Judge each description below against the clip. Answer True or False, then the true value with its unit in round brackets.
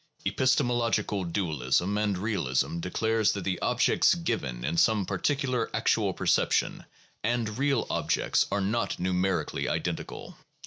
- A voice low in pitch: True (105 Hz)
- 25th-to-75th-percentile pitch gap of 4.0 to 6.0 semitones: True (4.6 semitones)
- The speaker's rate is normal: False (120 wpm)